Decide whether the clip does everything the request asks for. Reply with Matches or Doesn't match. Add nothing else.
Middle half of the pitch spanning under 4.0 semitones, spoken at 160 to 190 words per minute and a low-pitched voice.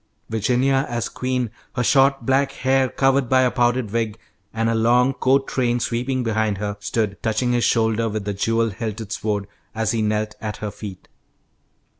Matches